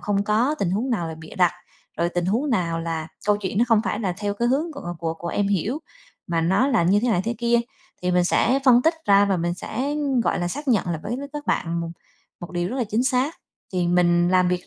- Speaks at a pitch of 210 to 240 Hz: No, high, 200 Hz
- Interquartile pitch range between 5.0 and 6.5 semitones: Yes, wide, 5.6 semitones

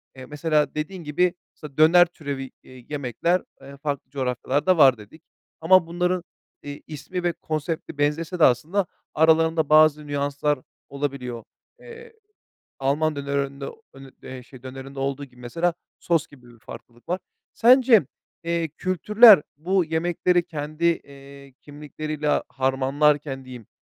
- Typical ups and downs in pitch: Yes, average, 3.6 semitones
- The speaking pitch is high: No, medium, 150 Hz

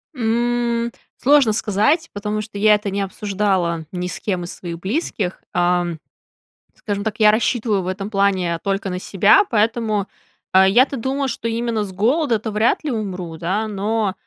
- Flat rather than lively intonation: No, average, 3.3 semitones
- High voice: Yes, high, 210 Hz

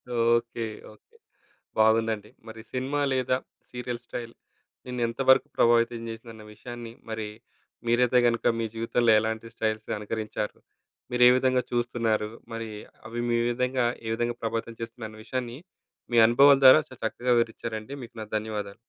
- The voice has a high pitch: No, low, 115 Hz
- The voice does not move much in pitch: Yes, narrow, 1.7 semitones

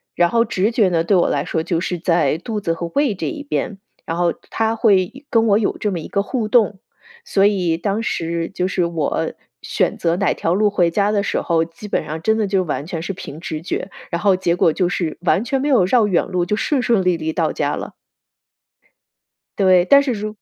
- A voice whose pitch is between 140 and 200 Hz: Yes, high, 190 Hz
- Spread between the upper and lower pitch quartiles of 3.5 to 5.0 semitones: Yes, average, 4.0 semitones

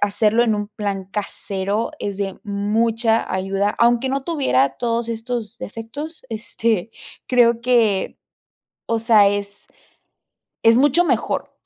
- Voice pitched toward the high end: Yes, high, 225 Hz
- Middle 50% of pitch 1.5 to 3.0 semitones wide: Yes, average, 2.7 semitones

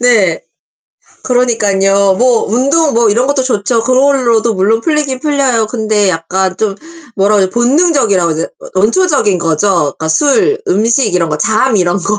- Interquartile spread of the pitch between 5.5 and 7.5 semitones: No, average, 5.1 semitones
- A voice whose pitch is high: Yes, high, 220 Hz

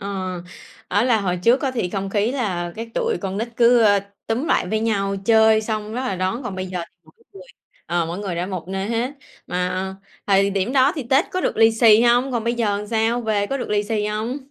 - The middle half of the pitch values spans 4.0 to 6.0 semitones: No, average, 3.5 semitones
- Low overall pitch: No, high, 215 Hz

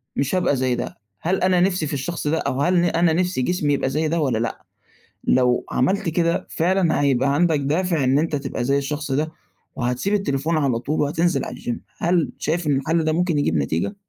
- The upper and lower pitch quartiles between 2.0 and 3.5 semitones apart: No, average, 4.1 semitones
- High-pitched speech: No, medium, 150 Hz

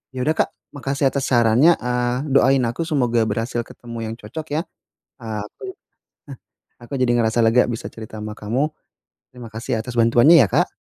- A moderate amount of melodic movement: Yes, average, 3.0 semitones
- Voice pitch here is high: No, low, 120 Hz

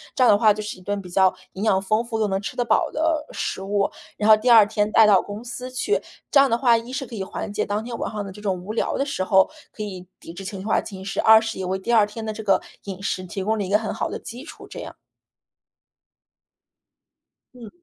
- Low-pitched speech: No, high, 210 Hz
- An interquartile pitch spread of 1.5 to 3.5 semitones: Yes, average, 2.9 semitones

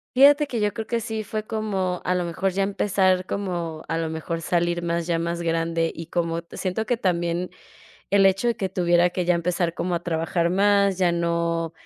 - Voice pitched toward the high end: No, medium, 180 Hz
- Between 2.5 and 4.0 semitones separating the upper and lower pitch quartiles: Yes, average, 2.8 semitones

